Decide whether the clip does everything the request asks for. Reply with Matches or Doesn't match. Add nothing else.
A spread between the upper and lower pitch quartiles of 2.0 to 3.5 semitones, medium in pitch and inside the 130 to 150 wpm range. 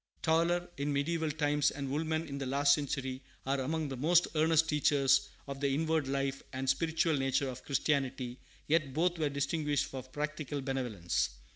Doesn't match